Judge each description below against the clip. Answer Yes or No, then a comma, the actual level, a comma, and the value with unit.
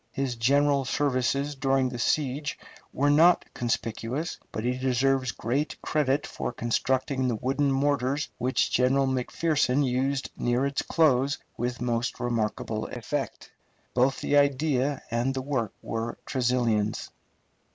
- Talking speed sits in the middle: No, slow, 130 wpm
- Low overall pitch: Yes, low, 130 Hz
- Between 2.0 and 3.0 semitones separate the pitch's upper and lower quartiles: Yes, narrow, 2.5 semitones